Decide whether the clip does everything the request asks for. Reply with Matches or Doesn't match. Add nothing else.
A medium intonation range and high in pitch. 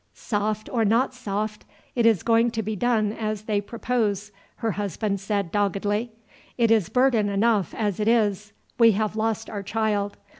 Doesn't match